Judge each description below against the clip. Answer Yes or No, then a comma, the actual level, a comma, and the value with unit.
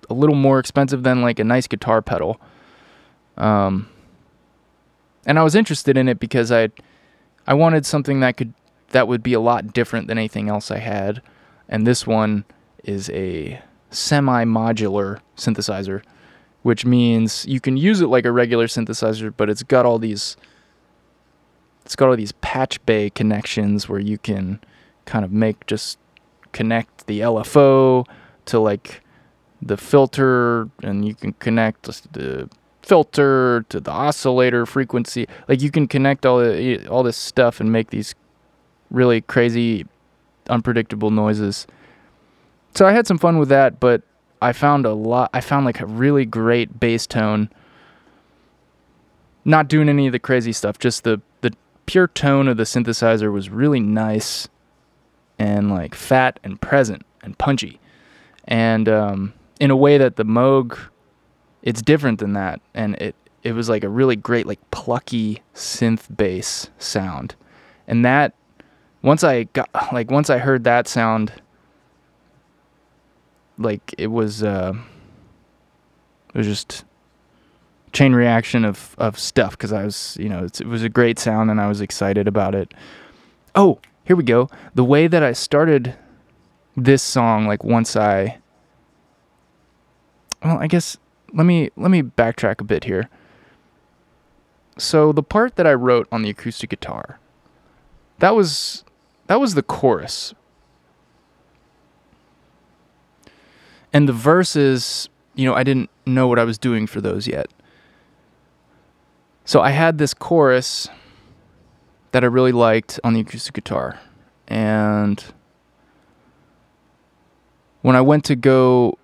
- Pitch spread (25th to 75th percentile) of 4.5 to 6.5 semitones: No, average, 3.8 semitones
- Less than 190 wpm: Yes, average, 145 wpm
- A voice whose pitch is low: Yes, low, 115 Hz